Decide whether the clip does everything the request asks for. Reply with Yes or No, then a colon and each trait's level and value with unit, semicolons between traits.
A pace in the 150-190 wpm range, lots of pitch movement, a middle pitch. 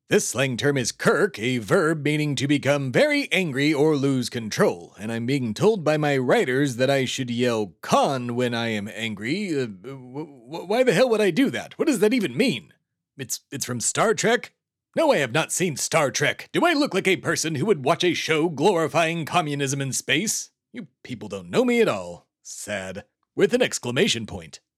No: fast, 205 wpm; wide, 5.7 semitones; medium, 145 Hz